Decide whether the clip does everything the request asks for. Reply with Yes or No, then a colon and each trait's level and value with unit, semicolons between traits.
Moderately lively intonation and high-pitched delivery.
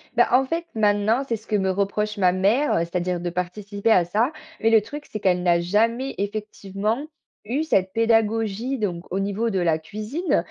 Yes: average, 3.4 semitones; high, 210 Hz